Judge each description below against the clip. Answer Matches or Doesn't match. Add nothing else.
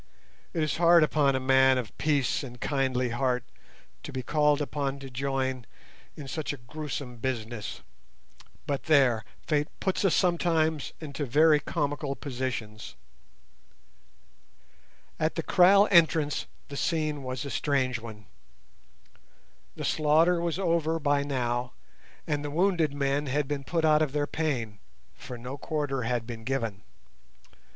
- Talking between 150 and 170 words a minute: Doesn't match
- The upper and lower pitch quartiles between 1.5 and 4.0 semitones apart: Matches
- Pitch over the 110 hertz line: Matches